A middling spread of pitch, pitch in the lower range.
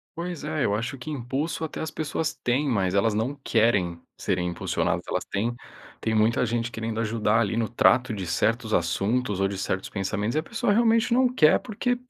No: wide, 6.6 semitones; low, 115 Hz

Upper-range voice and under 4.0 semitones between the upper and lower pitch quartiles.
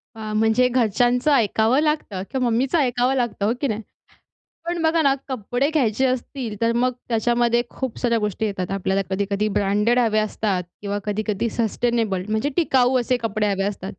Yes: high, 230 Hz; average, 3.3 semitones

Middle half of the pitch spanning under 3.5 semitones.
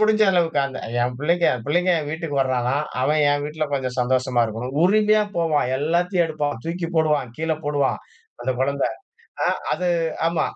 No: average, 4.3 semitones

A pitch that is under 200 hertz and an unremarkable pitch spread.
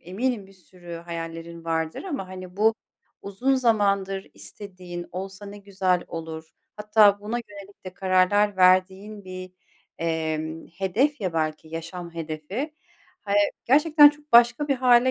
Yes: high, 190 Hz; average, 3.8 semitones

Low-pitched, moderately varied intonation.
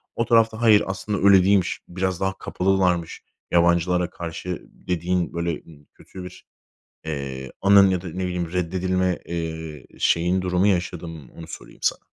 No: very low, 90 Hz; narrow, 2.1 semitones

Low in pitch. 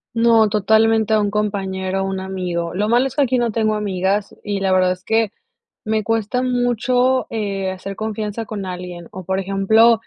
No: high, 210 Hz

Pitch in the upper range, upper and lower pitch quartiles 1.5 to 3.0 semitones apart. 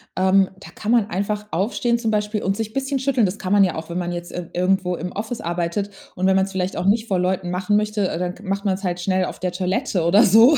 Yes: high, 195 Hz; average, 2.7 semitones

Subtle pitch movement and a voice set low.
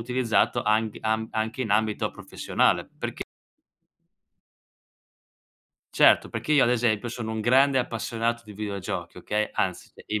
Yes: narrow, 2.0 semitones; low, 110 Hz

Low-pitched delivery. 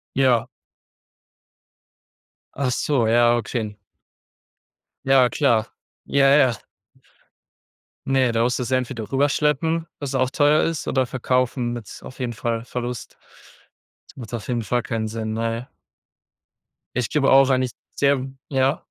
Yes: low, 125 Hz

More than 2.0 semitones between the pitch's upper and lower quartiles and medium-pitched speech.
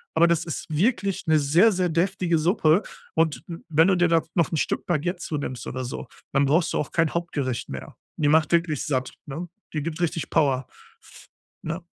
Yes: average, 2.7 semitones; medium, 160 Hz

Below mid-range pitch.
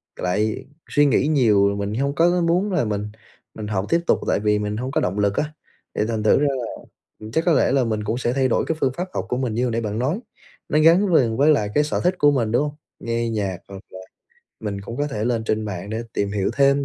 Yes: low, 115 Hz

